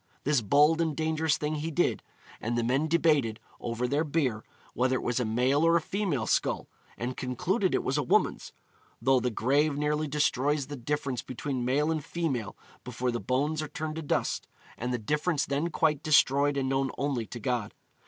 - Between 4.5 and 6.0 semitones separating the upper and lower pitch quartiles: No, average, 3.6 semitones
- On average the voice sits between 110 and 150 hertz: Yes, medium, 140 Hz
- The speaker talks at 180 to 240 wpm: Yes, average, 190 wpm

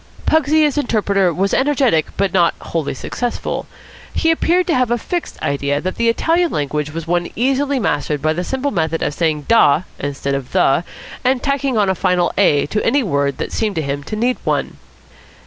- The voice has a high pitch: Yes, high, 195 Hz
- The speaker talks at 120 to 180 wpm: No, average, 195 wpm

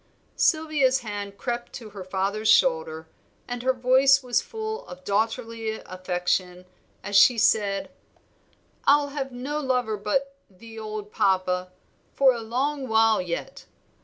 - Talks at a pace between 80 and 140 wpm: Yes, slow, 135 wpm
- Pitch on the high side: Yes, high, 225 Hz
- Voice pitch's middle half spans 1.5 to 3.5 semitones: No, average, 4.9 semitones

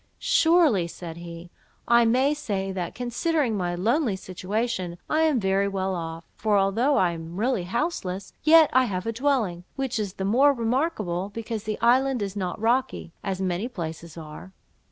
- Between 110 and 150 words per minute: No, average, 170 wpm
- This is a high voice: Yes, high, 205 Hz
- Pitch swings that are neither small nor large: No, wide, 5.7 semitones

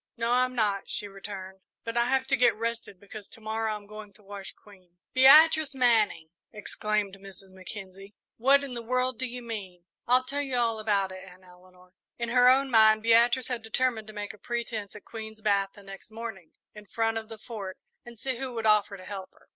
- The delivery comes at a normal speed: No, fast, 210 wpm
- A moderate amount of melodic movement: Yes, average, 3.3 semitones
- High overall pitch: Yes, high, 220 Hz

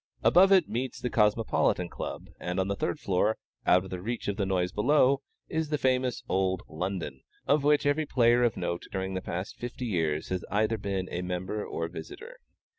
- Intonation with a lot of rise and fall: Yes, wide, 5.8 semitones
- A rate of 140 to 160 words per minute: No, average, 190 wpm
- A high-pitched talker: No, low, 105 Hz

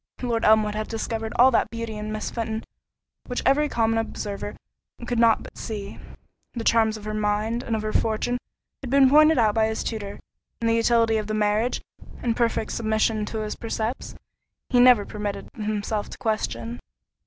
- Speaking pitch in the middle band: No, high, 220 Hz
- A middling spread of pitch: No, narrow, 1.6 semitones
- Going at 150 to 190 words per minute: Yes, average, 180 wpm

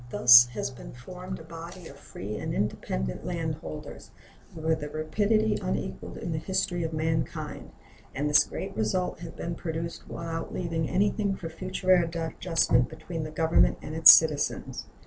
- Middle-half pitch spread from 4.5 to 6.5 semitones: No, average, 2.8 semitones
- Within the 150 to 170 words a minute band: Yes, average, 155 wpm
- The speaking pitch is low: No, medium, 160 Hz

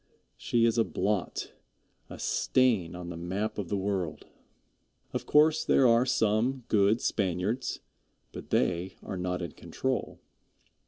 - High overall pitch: No, low, 105 Hz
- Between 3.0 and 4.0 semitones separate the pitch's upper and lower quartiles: No, average, 4.6 semitones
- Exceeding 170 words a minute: No, average, 140 wpm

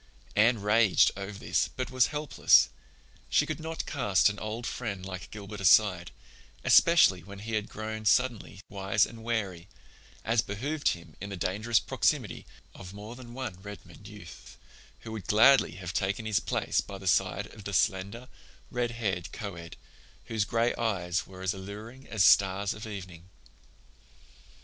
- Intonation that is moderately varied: Yes, average, 3.3 semitones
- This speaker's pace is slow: No, average, 160 wpm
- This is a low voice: Yes, low, 105 Hz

